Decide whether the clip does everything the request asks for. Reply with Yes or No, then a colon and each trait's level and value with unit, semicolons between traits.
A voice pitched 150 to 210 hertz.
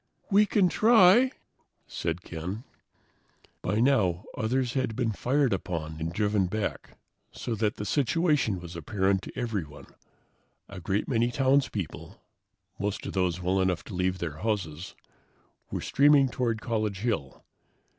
No: low, 105 Hz